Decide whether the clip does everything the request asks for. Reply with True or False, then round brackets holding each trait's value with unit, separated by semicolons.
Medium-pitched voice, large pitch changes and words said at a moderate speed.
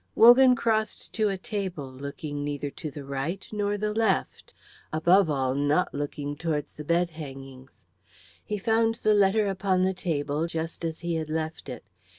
True (165 Hz; 5.8 semitones; 165 wpm)